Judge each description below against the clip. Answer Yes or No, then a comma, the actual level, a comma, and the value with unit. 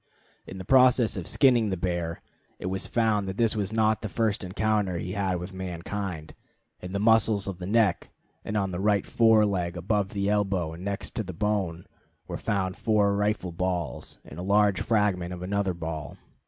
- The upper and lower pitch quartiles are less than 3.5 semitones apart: Yes, average, 2.7 semitones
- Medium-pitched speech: No, low, 100 Hz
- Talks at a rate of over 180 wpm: Yes, average, 195 wpm